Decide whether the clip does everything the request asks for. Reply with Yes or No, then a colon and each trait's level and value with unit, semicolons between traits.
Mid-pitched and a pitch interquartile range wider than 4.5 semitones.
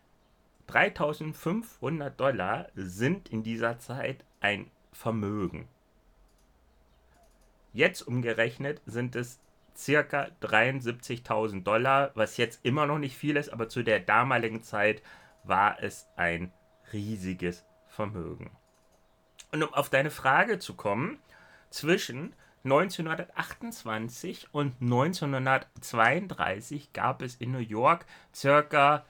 No: low, 125 Hz; average, 4.9 semitones